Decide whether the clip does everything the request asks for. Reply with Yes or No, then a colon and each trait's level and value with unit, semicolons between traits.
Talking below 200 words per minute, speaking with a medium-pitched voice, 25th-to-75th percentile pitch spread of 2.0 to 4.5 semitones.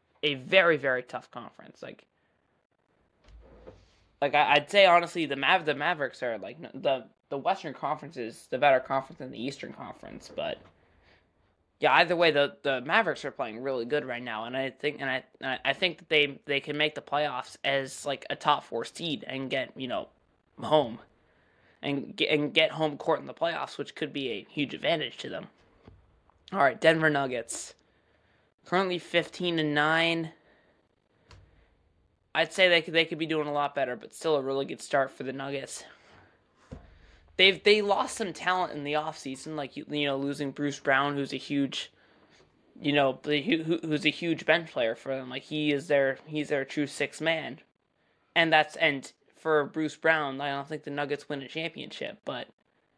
Yes: average, 185 wpm; medium, 145 Hz; average, 3.0 semitones